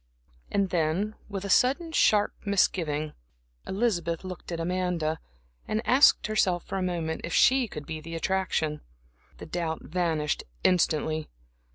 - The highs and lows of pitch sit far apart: No, average, 3.8 semitones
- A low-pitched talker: No, medium, 180 Hz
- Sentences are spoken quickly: No, average, 140 wpm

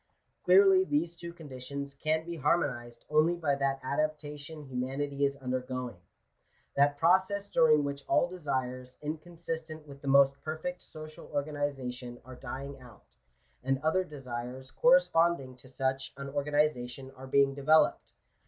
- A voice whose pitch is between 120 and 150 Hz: Yes, medium, 140 Hz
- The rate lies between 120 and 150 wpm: Yes, average, 140 wpm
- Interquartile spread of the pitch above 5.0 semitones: No, average, 3.1 semitones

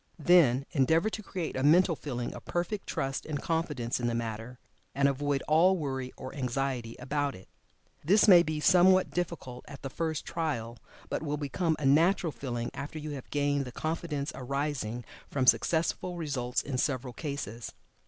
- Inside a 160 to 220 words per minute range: Yes, average, 170 wpm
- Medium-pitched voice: Yes, medium, 145 Hz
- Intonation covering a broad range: No, average, 4.2 semitones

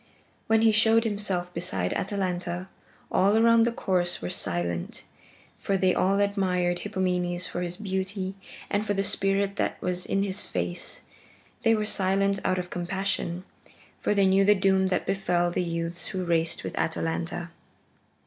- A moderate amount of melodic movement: No, narrow, 2.2 semitones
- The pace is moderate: Yes, average, 160 wpm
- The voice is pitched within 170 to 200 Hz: Yes, high, 190 Hz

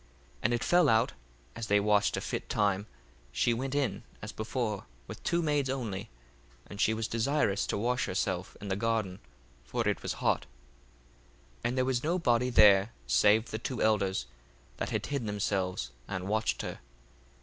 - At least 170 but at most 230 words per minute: Yes, average, 180 wpm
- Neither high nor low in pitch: No, low, 110 Hz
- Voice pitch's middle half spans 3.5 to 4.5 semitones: Yes, average, 3.8 semitones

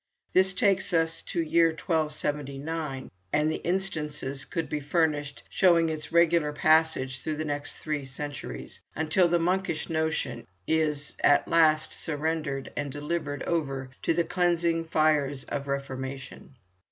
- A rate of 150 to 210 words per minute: No, average, 140 wpm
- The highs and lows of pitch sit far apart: No, narrow, 2.5 semitones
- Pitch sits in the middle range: Yes, medium, 155 Hz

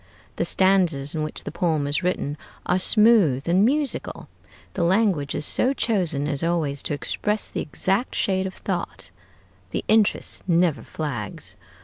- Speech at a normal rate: Yes, average, 150 wpm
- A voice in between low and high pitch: Yes, medium, 175 Hz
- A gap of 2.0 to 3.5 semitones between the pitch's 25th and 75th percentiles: No, average, 5.0 semitones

